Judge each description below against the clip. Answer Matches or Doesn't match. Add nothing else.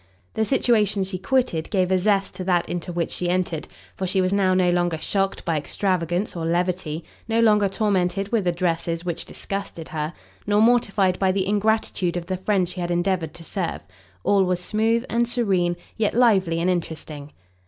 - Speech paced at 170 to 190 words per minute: Matches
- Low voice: Doesn't match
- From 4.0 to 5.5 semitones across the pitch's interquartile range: Doesn't match